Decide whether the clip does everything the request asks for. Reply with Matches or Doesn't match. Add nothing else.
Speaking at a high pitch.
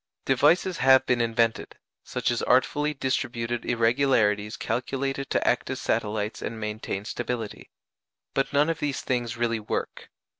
Doesn't match